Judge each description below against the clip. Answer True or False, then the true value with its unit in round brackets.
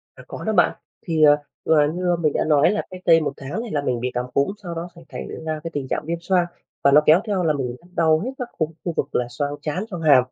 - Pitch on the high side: False (155 Hz)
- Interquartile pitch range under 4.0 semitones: True (3.5 semitones)